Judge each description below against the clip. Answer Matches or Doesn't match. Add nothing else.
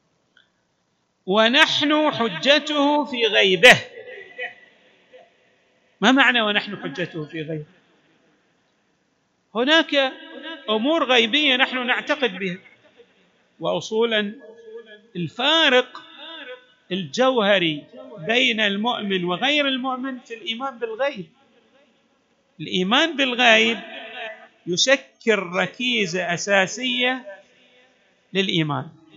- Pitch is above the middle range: Matches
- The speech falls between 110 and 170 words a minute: Doesn't match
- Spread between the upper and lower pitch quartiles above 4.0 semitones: Matches